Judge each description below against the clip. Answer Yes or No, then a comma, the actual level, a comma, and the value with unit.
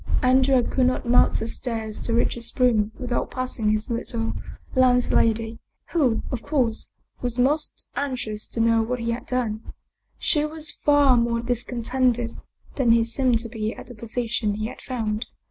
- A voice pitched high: Yes, high, 240 Hz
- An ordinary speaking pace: Yes, average, 165 wpm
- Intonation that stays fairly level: Yes, narrow, 2.0 semitones